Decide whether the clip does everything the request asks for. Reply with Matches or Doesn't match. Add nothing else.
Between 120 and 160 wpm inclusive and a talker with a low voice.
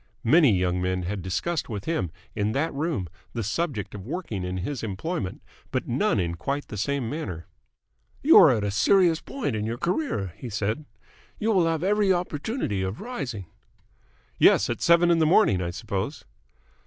Doesn't match